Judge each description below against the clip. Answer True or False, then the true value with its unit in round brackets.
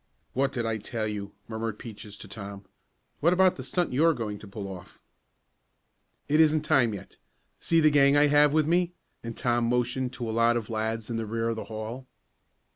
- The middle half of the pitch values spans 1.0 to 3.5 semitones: False (4.9 semitones)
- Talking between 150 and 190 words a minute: False (205 wpm)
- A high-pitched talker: False (115 Hz)